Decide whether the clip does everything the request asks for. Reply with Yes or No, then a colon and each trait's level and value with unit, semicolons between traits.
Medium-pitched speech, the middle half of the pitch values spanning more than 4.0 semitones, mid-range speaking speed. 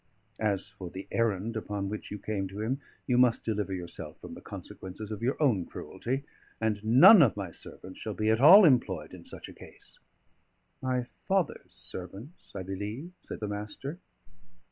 No: low, 105 Hz; average, 4.4 semitones; average, 175 wpm